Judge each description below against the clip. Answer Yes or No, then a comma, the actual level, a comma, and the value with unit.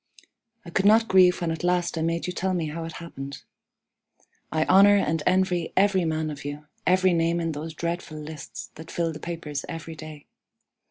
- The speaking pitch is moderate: Yes, medium, 165 Hz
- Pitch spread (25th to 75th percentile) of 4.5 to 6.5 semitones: No, narrow, 2.4 semitones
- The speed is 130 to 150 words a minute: No, average, 195 wpm